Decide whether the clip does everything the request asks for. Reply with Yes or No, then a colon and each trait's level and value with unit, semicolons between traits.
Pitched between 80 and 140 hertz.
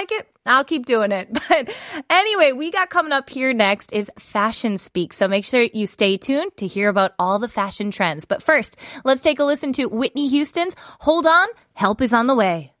No: very high, 255 Hz